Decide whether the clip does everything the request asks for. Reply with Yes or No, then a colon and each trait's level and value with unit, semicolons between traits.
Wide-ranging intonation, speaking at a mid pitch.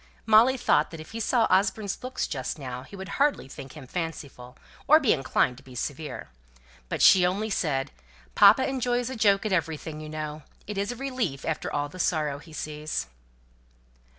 Yes: wide, 6.8 semitones; medium, 165 Hz